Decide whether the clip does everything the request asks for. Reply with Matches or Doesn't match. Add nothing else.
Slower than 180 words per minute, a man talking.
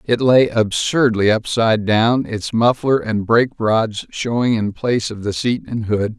Matches